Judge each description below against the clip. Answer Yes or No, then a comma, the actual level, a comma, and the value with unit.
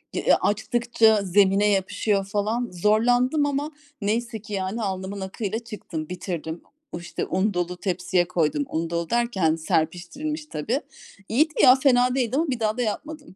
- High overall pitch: Yes, high, 210 Hz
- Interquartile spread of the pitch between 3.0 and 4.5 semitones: No, average, 5.2 semitones